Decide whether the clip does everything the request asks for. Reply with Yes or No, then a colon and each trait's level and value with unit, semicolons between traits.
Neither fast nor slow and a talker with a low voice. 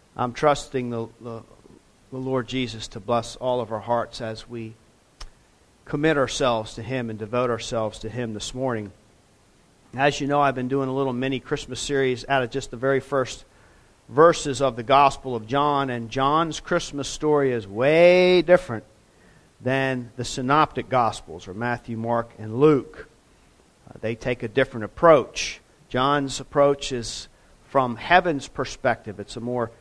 Yes: average, 160 wpm; low, 125 Hz